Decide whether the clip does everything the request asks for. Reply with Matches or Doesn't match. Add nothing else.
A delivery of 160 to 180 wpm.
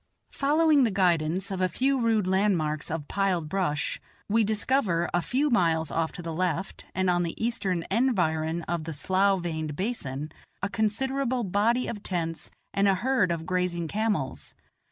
Matches